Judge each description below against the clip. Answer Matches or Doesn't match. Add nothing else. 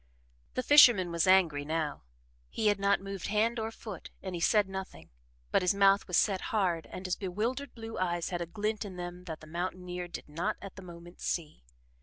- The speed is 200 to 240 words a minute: Matches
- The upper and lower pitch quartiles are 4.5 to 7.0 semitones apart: Doesn't match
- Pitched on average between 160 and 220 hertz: Matches